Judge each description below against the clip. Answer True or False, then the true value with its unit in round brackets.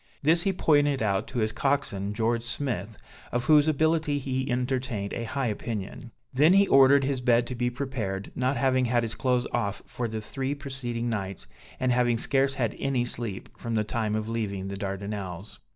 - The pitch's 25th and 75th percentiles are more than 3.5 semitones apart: True (3.9 semitones)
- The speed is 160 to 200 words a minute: True (185 wpm)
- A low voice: True (120 Hz)